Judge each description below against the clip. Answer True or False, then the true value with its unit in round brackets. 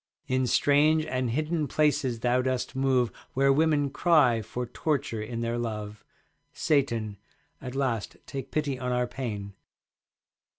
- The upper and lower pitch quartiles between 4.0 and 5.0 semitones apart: False (3.5 semitones)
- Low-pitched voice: True (130 Hz)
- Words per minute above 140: False (135 wpm)